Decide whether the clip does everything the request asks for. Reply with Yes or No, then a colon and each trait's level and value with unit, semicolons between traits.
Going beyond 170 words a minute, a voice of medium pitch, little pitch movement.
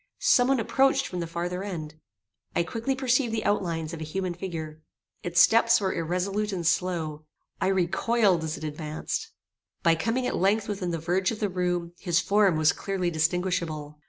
No: average, 180 wpm; medium, 180 Hz; average, 3.8 semitones